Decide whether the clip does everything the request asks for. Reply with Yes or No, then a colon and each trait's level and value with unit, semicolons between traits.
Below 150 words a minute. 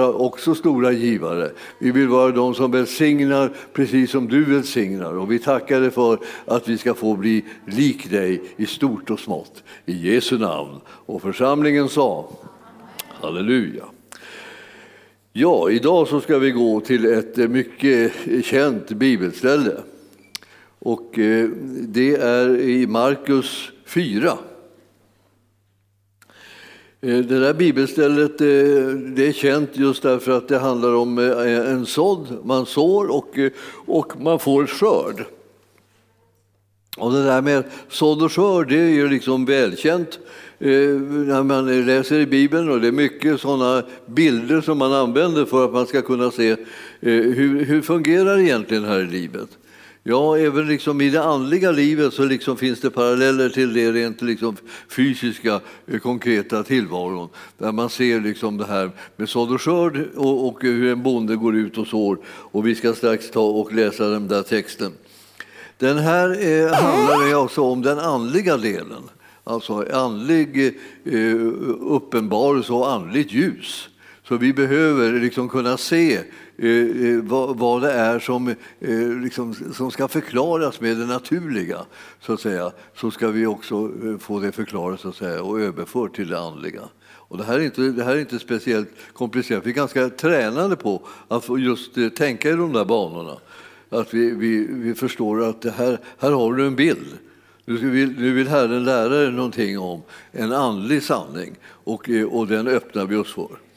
No: average, 155 wpm